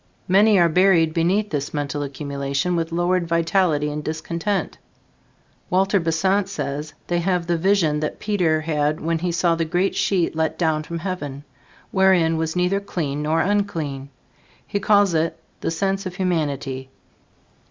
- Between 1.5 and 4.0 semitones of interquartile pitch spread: Yes, average, 3.5 semitones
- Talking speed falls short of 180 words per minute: Yes, average, 155 wpm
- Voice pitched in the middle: Yes, medium, 165 Hz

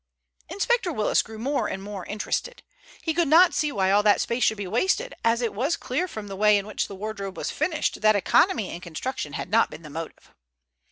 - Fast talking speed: Yes, fast, 220 wpm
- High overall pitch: Yes, high, 215 Hz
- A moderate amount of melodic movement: No, wide, 6.9 semitones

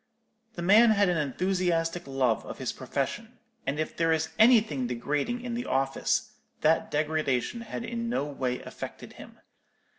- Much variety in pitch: Yes, wide, 7.7 semitones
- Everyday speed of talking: Yes, average, 155 wpm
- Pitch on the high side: No, medium, 165 Hz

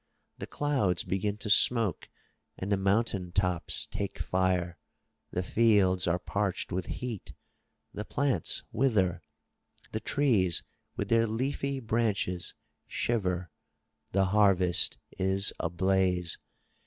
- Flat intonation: No, average, 3.6 semitones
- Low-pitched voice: Yes, very low, 95 Hz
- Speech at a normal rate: No, slow, 110 wpm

